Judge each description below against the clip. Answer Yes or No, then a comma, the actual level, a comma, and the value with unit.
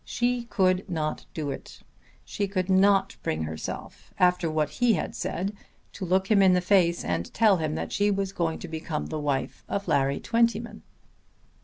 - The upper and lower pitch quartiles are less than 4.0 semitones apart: No, average, 4.3 semitones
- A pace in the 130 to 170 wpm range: No, average, 180 wpm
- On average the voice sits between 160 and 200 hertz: Yes, medium, 185 Hz